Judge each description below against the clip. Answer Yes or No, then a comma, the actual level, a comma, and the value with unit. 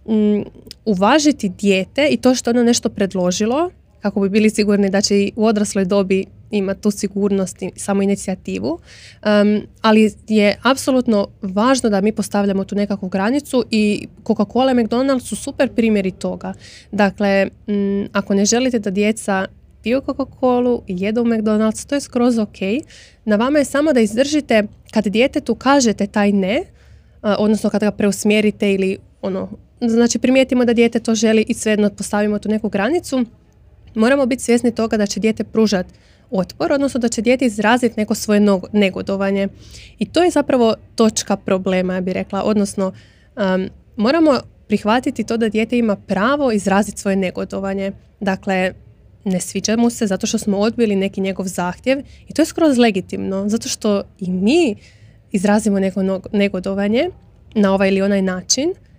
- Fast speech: Yes, fast, 165 wpm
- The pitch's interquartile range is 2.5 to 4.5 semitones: Yes, average, 3.2 semitones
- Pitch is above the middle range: Yes, high, 210 Hz